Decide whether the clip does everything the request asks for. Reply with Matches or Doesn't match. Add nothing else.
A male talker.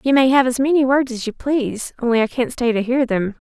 Doesn't match